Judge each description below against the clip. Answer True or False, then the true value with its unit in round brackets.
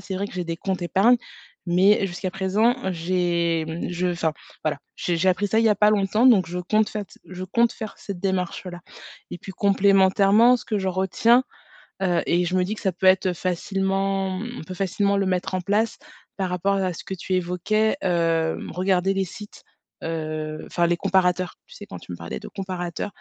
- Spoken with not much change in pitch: True (2.1 semitones)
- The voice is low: False (190 Hz)